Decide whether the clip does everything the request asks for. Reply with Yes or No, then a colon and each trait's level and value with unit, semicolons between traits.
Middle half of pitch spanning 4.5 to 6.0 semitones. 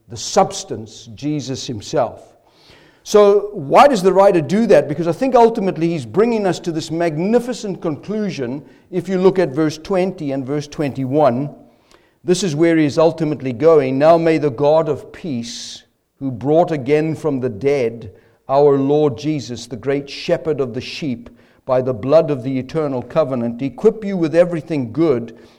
Yes: average, 4.8 semitones